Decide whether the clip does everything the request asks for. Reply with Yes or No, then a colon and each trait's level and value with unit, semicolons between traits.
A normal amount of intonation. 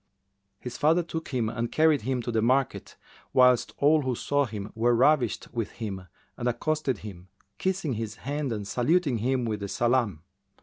Yes: average, 4.2 semitones